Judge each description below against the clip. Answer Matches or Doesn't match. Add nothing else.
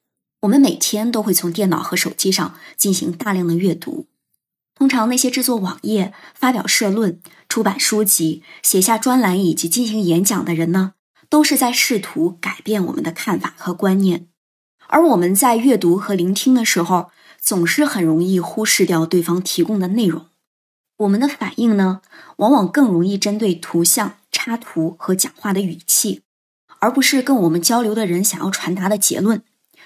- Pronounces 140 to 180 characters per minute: Doesn't match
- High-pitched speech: Matches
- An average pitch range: Matches